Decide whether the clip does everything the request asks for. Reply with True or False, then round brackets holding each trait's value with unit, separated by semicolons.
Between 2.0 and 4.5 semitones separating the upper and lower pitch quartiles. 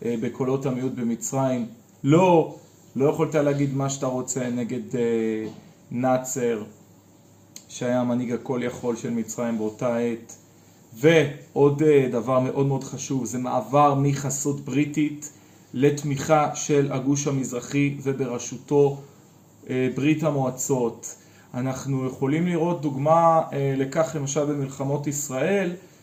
True (3.0 semitones)